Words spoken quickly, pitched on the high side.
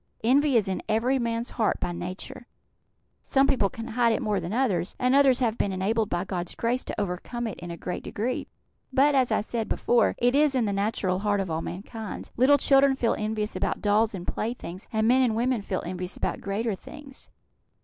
Yes: fast, 210 wpm; high, 225 Hz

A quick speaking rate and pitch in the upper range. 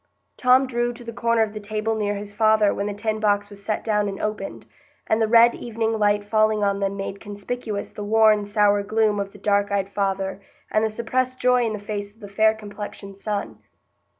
Yes: fast, 215 wpm; high, 210 Hz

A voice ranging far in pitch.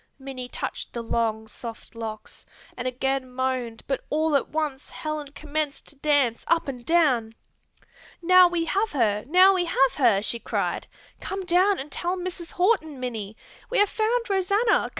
Yes: wide, 6.4 semitones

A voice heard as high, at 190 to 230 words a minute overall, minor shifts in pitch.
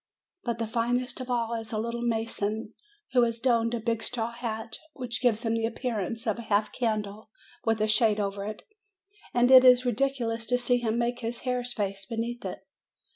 Yes: high, 230 Hz; average, 200 wpm; narrow, 1.8 semitones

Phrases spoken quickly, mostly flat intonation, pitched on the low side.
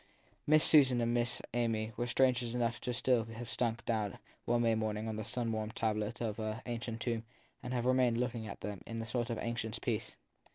Yes: fast, 215 wpm; narrow, 1.6 semitones; low, 115 Hz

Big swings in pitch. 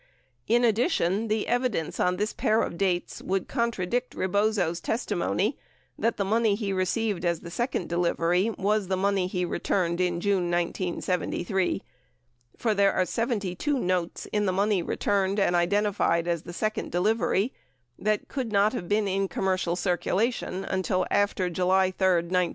No: average, 3.0 semitones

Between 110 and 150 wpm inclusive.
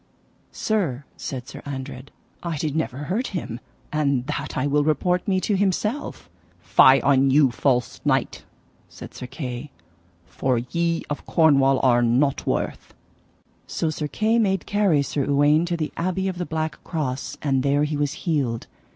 No: average, 160 wpm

